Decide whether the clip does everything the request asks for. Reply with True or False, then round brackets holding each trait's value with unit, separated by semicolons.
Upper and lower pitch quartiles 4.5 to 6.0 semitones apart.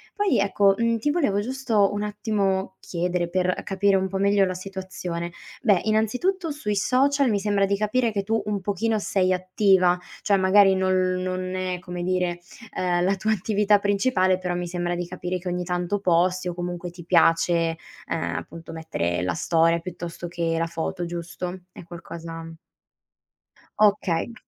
False (2.7 semitones)